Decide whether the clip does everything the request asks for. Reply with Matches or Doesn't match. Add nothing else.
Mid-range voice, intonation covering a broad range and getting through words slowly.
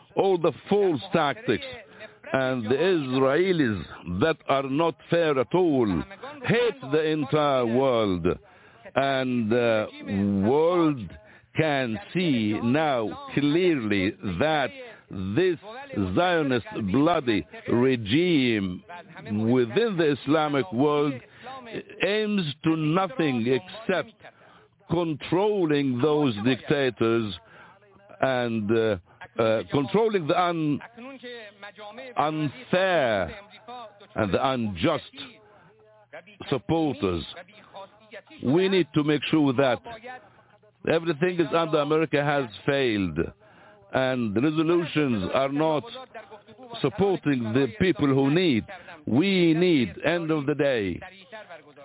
Matches